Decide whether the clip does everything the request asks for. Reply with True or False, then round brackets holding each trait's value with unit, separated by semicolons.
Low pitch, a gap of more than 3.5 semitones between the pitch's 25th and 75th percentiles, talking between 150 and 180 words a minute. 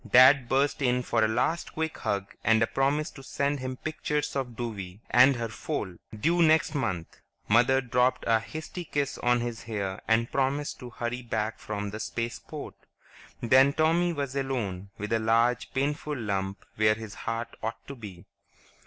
True (120 Hz; 4.0 semitones; 170 wpm)